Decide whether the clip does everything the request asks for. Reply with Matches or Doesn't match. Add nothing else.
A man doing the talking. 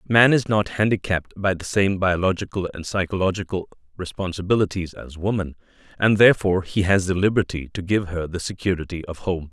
Matches